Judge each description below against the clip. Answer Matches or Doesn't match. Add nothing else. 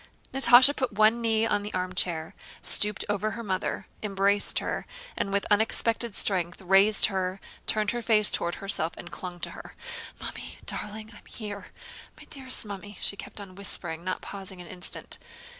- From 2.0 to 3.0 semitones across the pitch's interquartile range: Matches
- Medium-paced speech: Matches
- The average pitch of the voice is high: Matches